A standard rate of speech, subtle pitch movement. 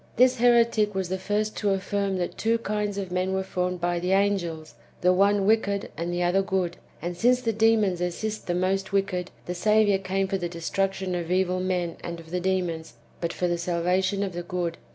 No: fast, 215 wpm; narrow, 2.3 semitones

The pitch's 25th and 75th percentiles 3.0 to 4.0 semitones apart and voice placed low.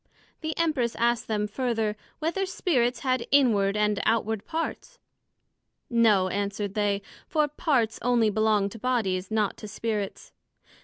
No: average, 3.7 semitones; high, 225 Hz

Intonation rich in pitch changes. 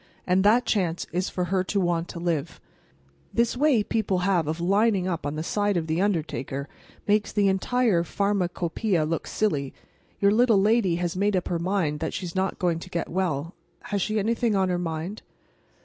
No: average, 3.4 semitones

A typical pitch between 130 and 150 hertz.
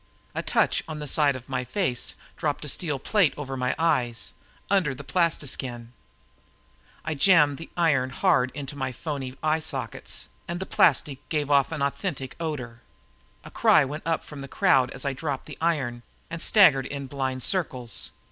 Yes: medium, 140 Hz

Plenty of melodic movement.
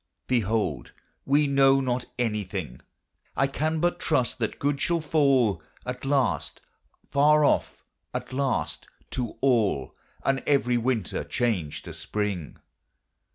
No: average, 4.6 semitones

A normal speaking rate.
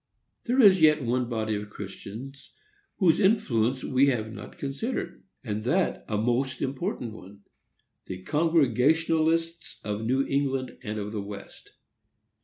No: slow, 130 wpm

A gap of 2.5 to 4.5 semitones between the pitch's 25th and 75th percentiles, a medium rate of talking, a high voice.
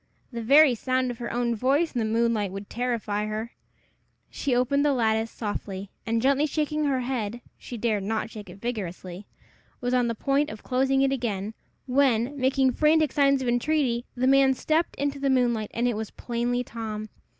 Yes: average, 3.6 semitones; average, 185 wpm; high, 245 Hz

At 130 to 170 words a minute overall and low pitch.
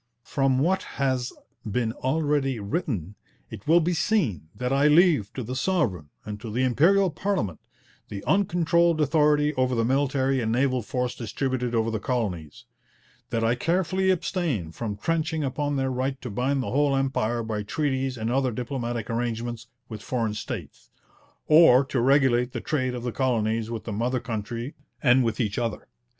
Yes: average, 165 wpm; low, 130 Hz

